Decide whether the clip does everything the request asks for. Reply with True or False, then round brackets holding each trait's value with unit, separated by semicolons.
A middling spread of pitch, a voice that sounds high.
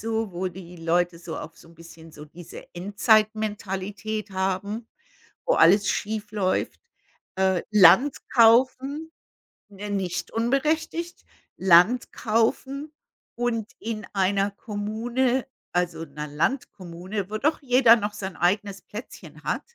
True (4.1 semitones; 205 Hz)